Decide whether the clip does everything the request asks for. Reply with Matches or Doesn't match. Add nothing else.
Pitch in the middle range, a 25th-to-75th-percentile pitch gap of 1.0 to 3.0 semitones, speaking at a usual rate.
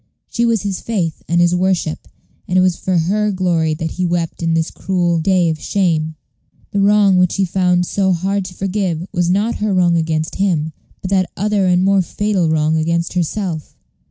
Matches